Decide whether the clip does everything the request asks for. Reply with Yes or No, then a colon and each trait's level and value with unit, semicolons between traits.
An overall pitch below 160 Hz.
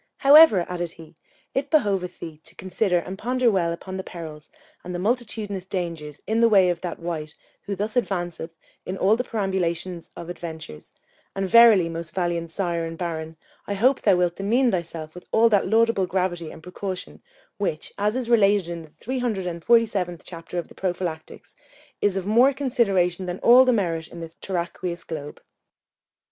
No: medium, 185 Hz